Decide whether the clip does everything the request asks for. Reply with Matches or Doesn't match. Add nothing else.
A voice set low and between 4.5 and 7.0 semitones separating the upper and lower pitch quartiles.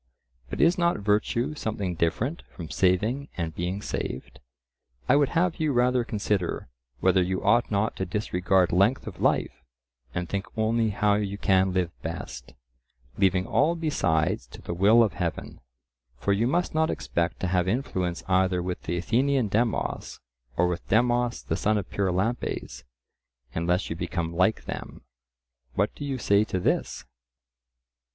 Matches